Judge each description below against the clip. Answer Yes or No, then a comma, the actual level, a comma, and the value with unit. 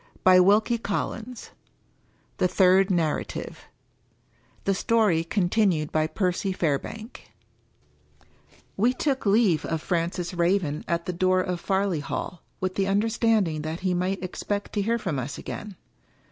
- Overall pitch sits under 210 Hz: Yes, medium, 185 Hz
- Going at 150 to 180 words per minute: No, slow, 135 wpm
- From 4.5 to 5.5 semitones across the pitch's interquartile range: No, average, 3.3 semitones